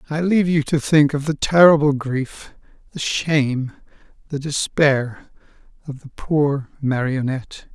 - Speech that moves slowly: Yes, slow, 130 wpm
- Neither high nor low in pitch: Yes, medium, 145 Hz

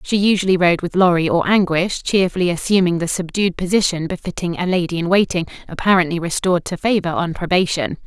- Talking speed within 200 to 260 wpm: No, average, 170 wpm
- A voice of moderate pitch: Yes, medium, 180 Hz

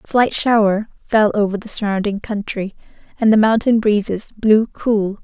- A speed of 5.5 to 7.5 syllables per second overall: No, 4.7 syllables/s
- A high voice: Yes, high, 210 Hz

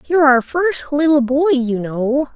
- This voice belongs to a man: No, female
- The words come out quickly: No, average, 180 wpm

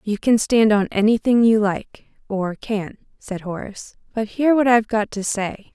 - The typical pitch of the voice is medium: No, high, 215 Hz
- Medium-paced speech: Yes, average, 175 wpm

